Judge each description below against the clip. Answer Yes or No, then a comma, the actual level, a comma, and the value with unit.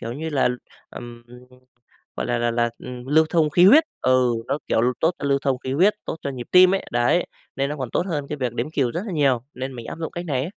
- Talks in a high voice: No, medium, 140 Hz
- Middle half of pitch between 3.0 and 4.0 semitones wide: No, average, 4.6 semitones